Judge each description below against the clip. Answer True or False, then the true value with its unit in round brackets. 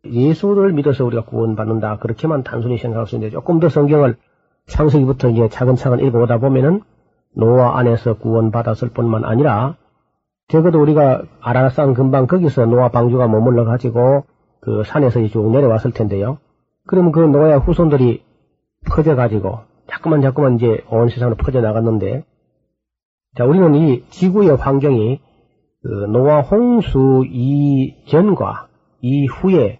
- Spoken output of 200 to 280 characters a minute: False (330 characters per minute)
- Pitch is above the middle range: False (130 Hz)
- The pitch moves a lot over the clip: False (4.1 semitones)